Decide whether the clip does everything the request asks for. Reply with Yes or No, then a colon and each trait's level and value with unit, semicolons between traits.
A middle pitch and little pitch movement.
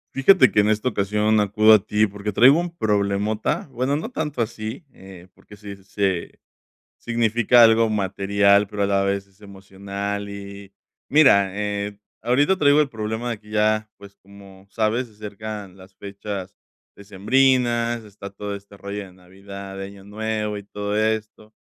No: low, 105 Hz; narrow, 1.9 semitones